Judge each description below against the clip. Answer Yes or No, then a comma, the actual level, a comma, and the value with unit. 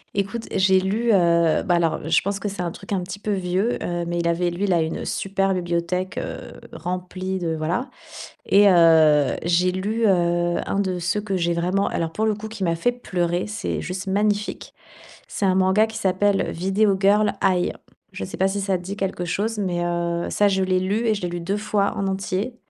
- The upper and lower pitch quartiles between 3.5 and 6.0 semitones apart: No, average, 2.7 semitones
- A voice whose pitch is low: No, high, 190 Hz